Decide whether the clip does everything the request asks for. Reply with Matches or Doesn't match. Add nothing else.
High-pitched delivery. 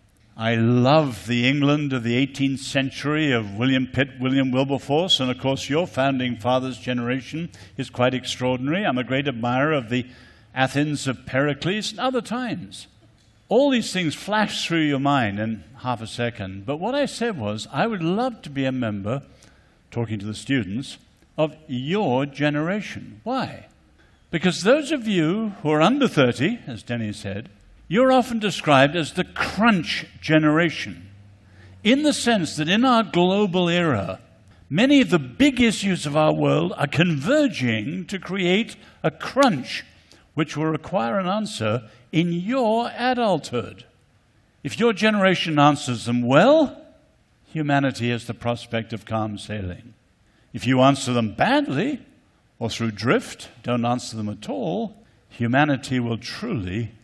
Doesn't match